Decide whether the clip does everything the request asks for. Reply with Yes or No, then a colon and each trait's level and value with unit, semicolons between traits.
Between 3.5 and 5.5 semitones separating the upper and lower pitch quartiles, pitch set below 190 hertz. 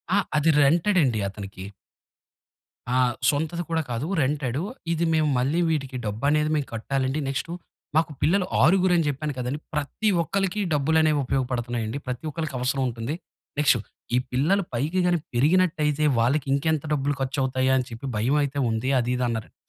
Yes: average, 3.9 semitones; medium, 140 Hz